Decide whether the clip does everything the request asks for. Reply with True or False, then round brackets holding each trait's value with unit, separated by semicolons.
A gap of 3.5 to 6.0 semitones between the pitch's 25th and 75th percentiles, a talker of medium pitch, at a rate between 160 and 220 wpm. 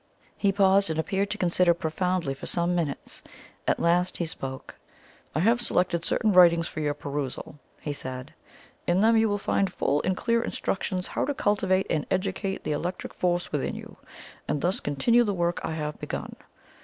True (3.9 semitones; 180 Hz; 180 wpm)